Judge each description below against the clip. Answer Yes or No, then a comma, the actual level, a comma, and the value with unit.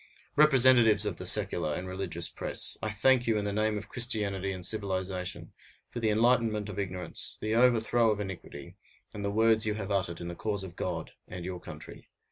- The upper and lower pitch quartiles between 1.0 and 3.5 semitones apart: Yes, average, 3.1 semitones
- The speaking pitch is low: Yes, low, 105 Hz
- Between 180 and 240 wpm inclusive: Yes, average, 195 wpm